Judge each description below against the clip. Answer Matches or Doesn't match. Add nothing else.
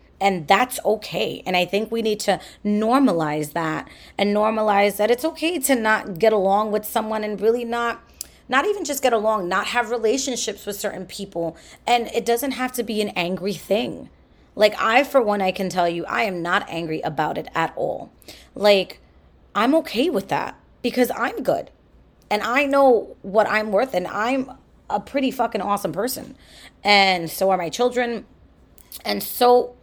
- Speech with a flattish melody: Doesn't match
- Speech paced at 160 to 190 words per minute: Matches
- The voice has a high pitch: Matches